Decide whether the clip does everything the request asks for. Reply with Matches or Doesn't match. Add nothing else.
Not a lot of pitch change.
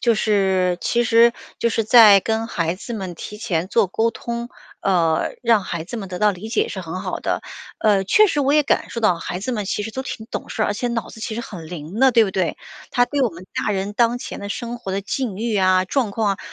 Doesn't match